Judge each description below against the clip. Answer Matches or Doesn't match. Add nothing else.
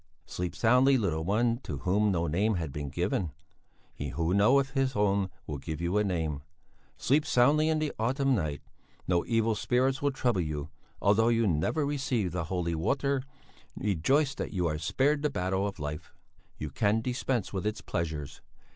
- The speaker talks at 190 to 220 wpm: Doesn't match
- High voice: Doesn't match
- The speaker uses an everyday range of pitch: Doesn't match